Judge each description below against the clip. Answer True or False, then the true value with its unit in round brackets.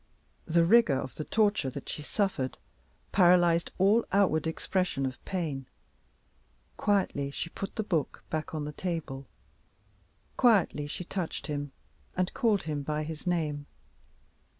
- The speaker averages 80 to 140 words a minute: True (135 wpm)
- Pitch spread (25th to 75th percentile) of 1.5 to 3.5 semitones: False (4.6 semitones)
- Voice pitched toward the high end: False (165 Hz)